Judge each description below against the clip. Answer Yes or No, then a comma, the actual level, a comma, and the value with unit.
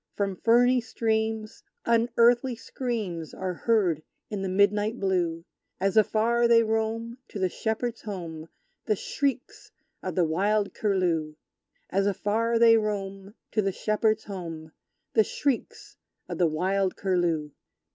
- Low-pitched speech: No, high, 210 Hz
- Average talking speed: No, slow, 130 wpm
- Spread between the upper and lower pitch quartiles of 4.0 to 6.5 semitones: No, average, 3.6 semitones